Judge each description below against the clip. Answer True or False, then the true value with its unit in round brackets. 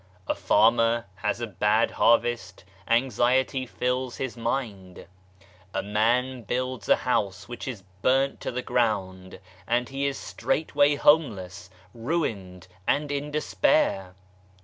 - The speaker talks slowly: True (125 wpm)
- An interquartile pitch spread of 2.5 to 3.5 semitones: False (4.1 semitones)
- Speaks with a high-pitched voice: False (120 Hz)